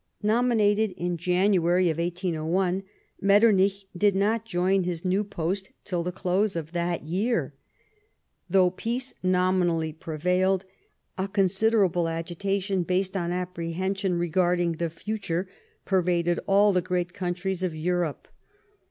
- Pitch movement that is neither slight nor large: No, narrow, 2.1 semitones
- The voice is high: No, medium, 180 Hz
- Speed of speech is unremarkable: No, slow, 115 wpm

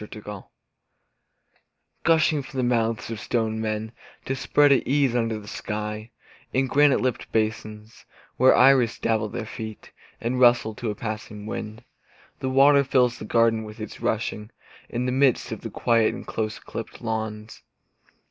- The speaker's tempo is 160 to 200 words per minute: Yes, average, 165 wpm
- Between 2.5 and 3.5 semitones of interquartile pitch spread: Yes, average, 3.0 semitones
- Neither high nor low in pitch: No, low, 115 Hz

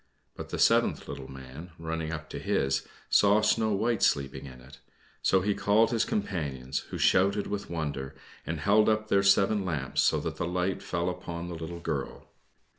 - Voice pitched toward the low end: Yes, very low, 85 Hz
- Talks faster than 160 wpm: Yes, average, 185 wpm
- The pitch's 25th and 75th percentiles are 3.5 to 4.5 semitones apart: No, wide, 5.5 semitones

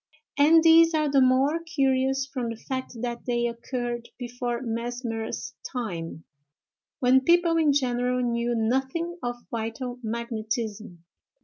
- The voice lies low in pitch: No, high, 245 Hz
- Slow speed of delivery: Yes, slow, 125 wpm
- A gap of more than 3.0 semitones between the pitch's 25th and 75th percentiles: No, narrow, 2.6 semitones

